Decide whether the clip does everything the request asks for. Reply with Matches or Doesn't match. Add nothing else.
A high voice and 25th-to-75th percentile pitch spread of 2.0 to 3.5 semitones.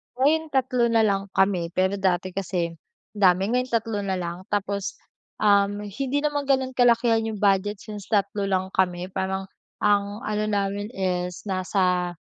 Matches